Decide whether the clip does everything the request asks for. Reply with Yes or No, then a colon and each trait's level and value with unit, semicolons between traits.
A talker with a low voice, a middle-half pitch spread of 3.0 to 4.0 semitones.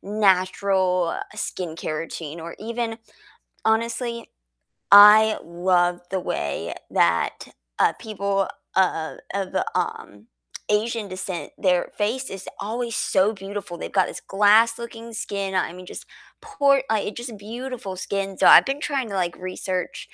No: high, 200 Hz; average, 3.7 semitones